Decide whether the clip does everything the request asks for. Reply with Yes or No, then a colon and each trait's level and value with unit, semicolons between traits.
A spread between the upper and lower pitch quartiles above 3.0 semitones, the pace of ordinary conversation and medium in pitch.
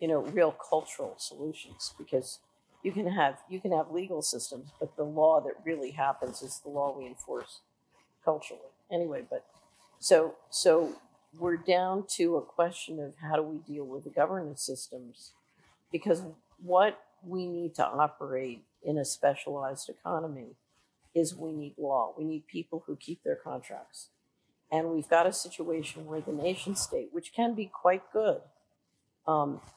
Yes: average, 3.6 semitones; average, 160 wpm; medium, 160 Hz